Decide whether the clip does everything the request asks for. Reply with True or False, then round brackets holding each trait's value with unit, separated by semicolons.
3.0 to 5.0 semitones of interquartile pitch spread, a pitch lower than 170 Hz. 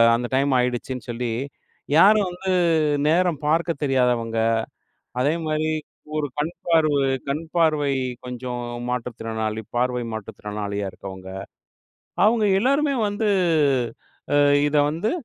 False (5.6 semitones; 140 Hz)